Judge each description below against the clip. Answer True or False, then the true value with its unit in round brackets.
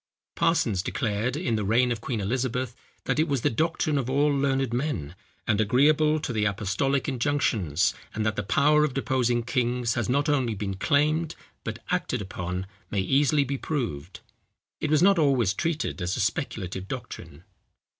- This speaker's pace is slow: False (170 wpm)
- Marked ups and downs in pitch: True (5.7 semitones)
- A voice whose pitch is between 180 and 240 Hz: False (125 Hz)